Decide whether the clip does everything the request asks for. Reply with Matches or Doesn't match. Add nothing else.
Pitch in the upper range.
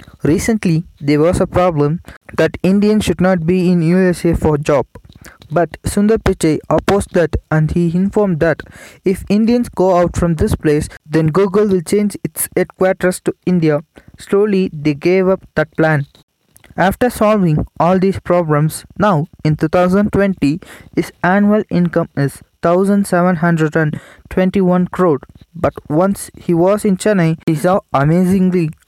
Doesn't match